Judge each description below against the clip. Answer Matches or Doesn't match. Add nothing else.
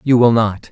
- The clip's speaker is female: Doesn't match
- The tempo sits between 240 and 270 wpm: Matches